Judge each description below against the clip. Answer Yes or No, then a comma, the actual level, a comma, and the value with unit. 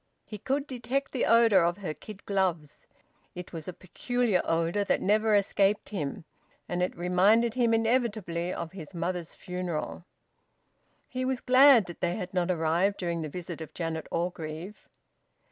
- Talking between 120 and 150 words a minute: No, average, 160 wpm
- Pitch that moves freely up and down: No, average, 4.6 semitones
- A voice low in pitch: No, medium, 185 Hz